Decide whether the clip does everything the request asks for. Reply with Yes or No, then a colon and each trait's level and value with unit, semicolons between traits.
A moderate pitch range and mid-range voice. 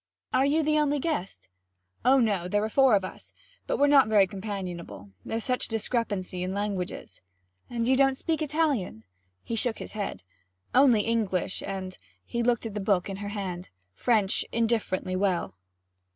No: average, 5.0 semitones; high, 215 Hz